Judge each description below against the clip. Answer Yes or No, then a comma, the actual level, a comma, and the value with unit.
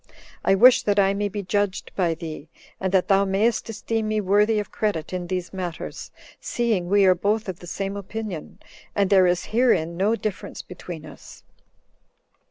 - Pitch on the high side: Yes, high, 195 Hz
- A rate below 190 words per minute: Yes, average, 175 wpm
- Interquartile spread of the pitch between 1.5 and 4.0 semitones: Yes, narrow, 2.6 semitones